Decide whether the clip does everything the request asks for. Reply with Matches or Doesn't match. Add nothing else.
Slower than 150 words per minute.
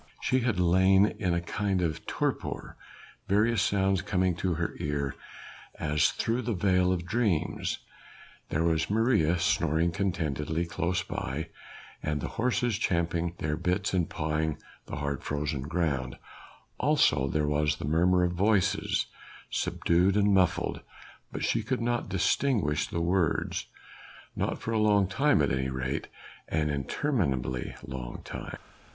Matches